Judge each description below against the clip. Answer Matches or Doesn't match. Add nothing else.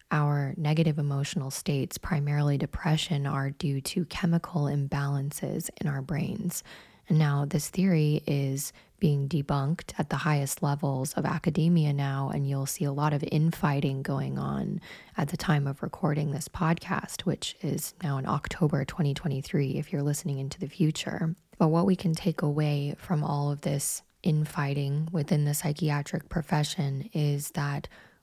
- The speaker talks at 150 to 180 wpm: Matches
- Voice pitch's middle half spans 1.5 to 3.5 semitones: Matches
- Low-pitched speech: Doesn't match